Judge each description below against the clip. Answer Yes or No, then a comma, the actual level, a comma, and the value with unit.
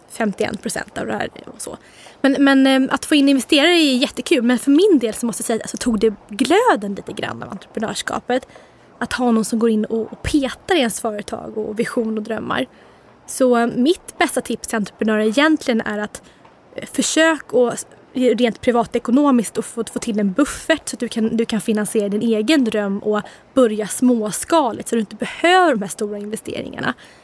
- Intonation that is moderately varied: Yes, average, 3.7 semitones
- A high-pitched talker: Yes, high, 235 Hz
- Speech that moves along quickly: No, average, 185 wpm